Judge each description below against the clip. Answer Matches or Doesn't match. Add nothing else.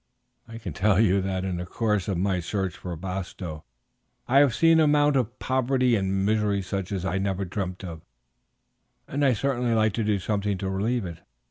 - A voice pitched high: Doesn't match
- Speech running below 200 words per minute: Doesn't match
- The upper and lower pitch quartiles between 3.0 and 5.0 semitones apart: Matches